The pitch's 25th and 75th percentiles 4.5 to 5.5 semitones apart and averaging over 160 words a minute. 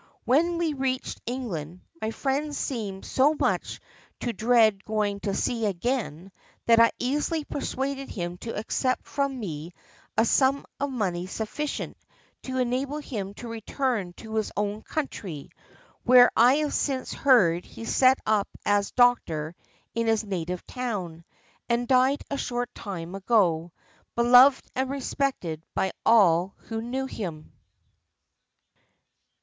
No: average, 5.2 semitones; slow, 135 wpm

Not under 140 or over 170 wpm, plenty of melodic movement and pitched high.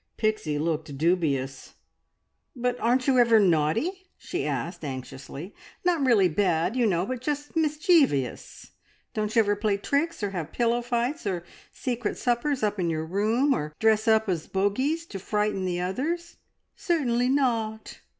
Yes: average, 150 wpm; wide, 6.4 semitones; high, 220 Hz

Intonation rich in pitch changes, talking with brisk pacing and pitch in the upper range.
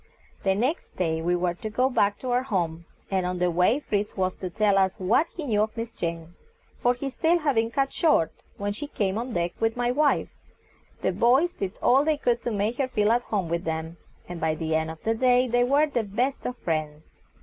Yes: wide, 6.0 semitones; fast, 240 wpm; high, 215 Hz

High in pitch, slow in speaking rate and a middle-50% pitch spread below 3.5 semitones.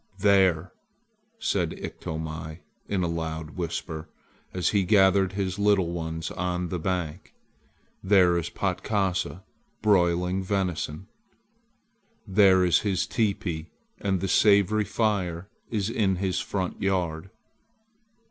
No: very low, 95 Hz; slow, 110 wpm; narrow, 2.5 semitones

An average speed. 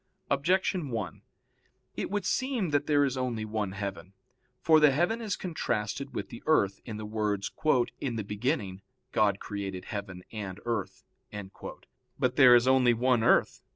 Yes: average, 155 wpm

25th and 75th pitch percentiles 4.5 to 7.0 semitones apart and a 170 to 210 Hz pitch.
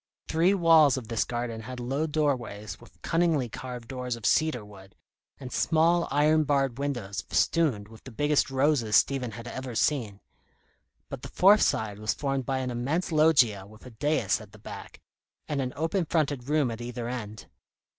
No: average, 4.8 semitones; low, 130 Hz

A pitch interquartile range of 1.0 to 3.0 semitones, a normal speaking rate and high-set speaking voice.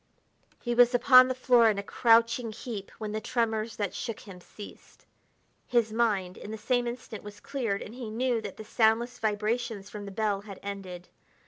Yes: average, 2.7 semitones; average, 190 wpm; high, 220 Hz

